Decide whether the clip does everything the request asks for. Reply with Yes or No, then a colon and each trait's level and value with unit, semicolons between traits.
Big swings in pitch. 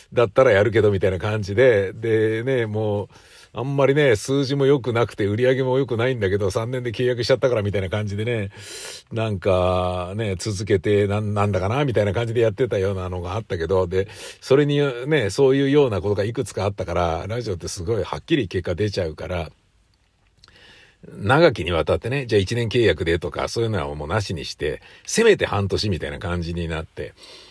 No: average, 4.0 semitones